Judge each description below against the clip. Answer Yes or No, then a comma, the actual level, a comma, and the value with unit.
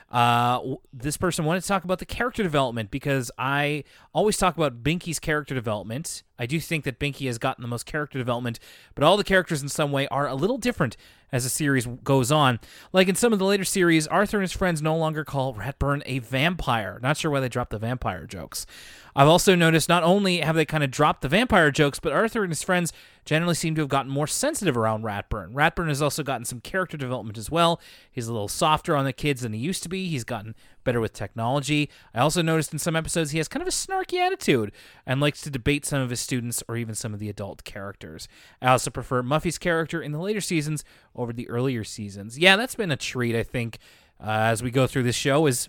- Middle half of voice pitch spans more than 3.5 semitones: Yes, average, 5.3 semitones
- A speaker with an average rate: No, fast, 235 wpm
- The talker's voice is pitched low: No, medium, 145 Hz